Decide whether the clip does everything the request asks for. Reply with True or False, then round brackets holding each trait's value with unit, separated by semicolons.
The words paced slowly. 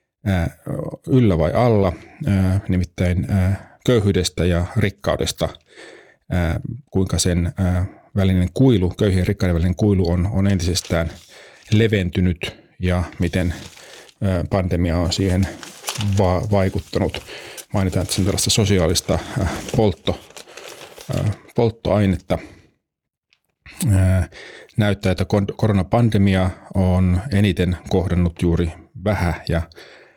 True (80 wpm)